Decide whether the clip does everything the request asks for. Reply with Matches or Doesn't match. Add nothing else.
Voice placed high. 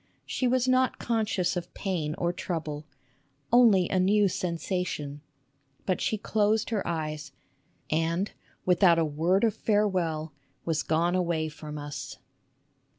Doesn't match